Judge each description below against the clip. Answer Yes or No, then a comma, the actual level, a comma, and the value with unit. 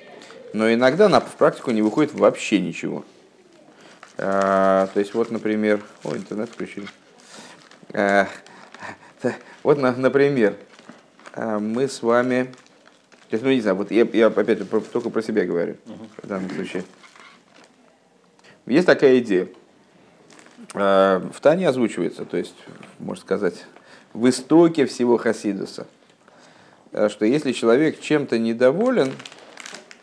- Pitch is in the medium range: No, low, 115 Hz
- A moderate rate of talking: No, slow, 105 wpm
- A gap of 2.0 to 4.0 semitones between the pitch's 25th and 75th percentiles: Yes, average, 3.6 semitones